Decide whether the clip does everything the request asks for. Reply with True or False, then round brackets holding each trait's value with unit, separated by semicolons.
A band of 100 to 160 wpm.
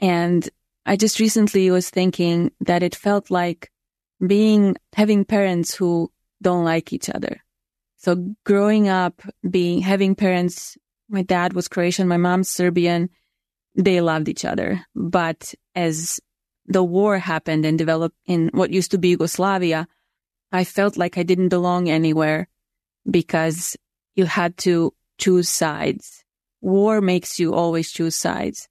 True (140 wpm)